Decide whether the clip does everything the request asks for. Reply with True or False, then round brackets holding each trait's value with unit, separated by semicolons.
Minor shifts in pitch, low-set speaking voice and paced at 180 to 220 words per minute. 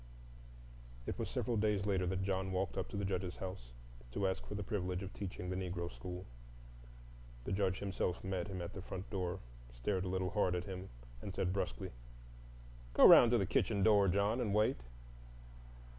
True (1.7 semitones; 95 Hz; 190 wpm)